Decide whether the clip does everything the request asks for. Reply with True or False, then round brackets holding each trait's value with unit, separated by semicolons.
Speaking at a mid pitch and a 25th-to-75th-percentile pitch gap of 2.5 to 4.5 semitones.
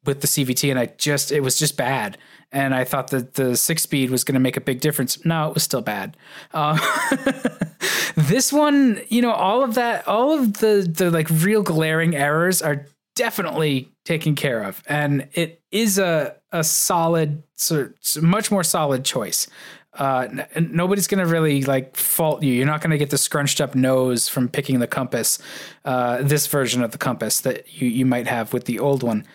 True (150 Hz; 4.0 semitones)